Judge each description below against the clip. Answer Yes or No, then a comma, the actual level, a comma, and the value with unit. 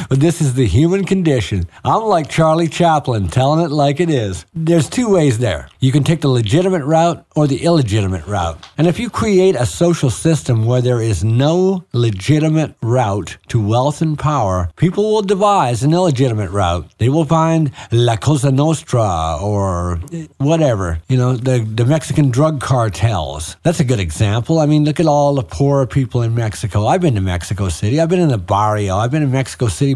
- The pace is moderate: Yes, average, 190 wpm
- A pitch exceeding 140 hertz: No, low, 135 Hz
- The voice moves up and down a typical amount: No, wide, 6.6 semitones